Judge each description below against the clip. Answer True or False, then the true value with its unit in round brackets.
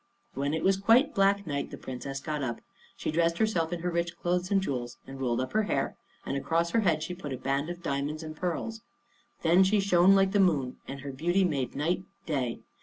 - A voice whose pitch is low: False (165 Hz)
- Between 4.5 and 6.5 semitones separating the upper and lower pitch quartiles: True (5.3 semitones)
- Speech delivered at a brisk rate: True (225 wpm)